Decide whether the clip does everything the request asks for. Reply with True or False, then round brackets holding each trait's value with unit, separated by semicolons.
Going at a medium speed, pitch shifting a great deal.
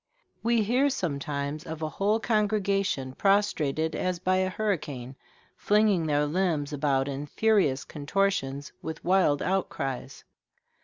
False (120 wpm; 5.7 semitones)